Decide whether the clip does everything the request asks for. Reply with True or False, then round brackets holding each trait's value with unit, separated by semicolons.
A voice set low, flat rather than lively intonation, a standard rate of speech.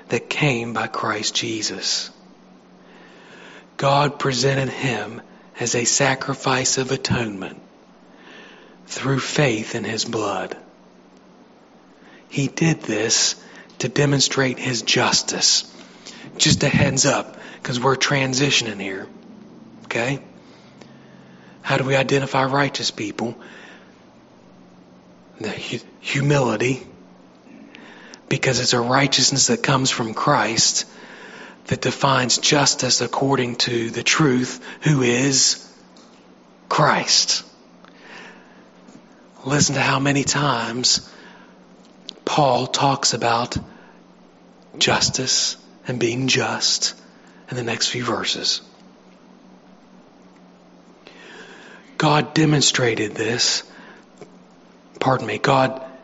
False (130 Hz; 2.2 semitones; 90 wpm)